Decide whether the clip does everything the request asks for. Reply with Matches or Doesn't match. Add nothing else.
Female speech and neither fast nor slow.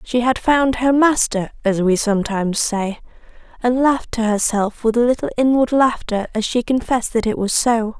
Matches